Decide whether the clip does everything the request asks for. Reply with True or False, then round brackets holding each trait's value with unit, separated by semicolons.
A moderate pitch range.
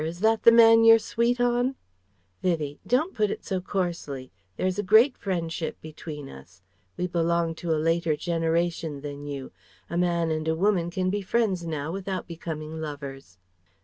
True (4.2 semitones)